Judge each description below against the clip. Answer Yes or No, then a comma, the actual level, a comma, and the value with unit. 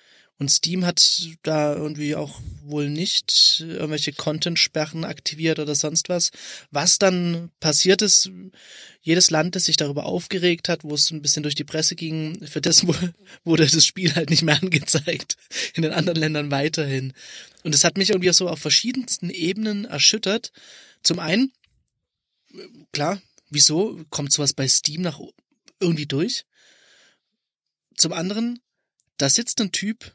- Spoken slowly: No, average, 150 wpm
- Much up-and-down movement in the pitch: No, average, 3.3 semitones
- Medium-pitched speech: Yes, medium, 165 Hz